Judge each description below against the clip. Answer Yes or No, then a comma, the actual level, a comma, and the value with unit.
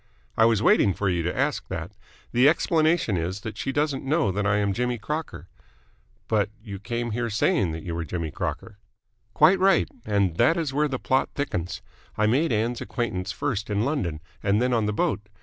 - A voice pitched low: Yes, low, 110 Hz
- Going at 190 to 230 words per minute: Yes, average, 200 wpm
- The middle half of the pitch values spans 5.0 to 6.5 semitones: Yes, average, 5.3 semitones